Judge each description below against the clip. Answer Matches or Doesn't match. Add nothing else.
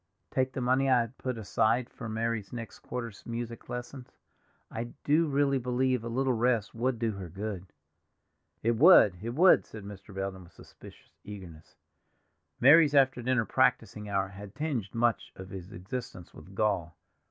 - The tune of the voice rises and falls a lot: Doesn't match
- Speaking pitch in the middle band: Doesn't match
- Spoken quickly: Doesn't match